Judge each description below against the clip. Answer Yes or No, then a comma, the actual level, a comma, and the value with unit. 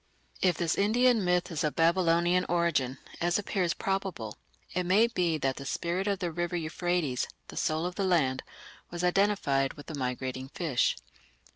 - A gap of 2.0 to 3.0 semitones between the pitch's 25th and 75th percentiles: No, average, 3.6 semitones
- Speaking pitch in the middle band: Yes, medium, 175 Hz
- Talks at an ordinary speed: Yes, average, 165 wpm